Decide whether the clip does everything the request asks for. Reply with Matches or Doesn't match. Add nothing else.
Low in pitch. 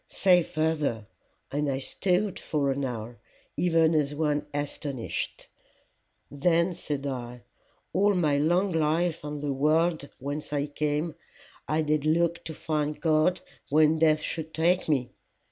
Doesn't match